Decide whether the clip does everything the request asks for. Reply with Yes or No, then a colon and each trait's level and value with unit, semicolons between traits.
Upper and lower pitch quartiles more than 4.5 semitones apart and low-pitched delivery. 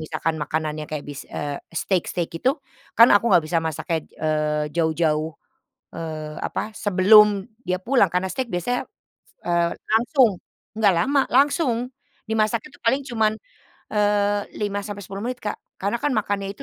No: wide, 5.6 semitones; high, 200 Hz